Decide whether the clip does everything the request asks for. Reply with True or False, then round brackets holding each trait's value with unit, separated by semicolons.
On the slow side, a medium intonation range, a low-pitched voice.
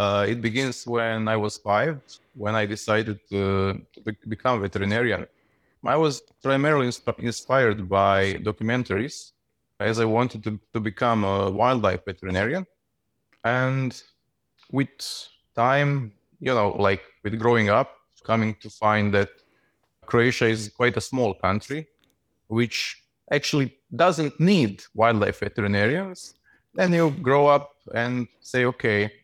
True (130 wpm; 3.9 semitones; 115 Hz)